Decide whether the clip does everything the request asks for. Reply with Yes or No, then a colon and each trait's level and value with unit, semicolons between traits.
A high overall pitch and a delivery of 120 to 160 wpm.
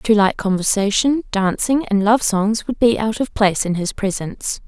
No: high, 210 Hz; average, 195 wpm